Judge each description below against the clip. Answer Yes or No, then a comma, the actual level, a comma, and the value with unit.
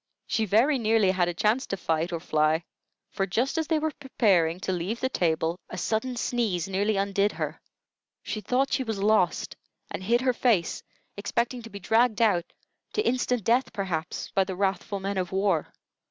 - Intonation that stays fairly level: No, average, 4.6 semitones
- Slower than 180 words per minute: No, average, 185 wpm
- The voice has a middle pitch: No, high, 200 Hz